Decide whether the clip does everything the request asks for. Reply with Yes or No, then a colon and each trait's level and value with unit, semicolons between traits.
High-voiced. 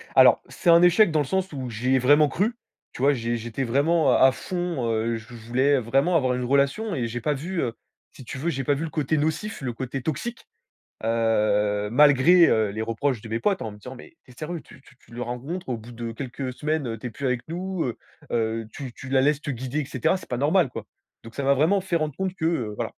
No: low, 135 Hz